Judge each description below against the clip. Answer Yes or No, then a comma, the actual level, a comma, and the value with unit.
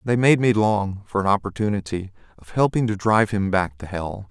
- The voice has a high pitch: No, low, 105 Hz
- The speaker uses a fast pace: Yes, fast, 210 wpm